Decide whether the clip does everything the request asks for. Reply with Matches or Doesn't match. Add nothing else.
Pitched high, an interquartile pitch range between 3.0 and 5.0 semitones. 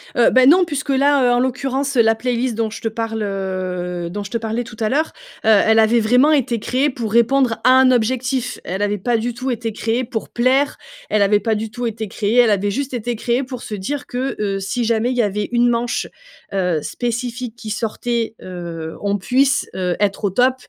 Matches